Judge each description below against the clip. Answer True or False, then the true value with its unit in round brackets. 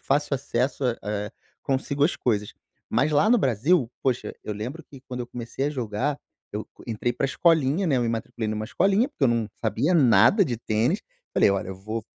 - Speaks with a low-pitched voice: True (125 Hz)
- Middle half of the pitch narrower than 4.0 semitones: False (4.9 semitones)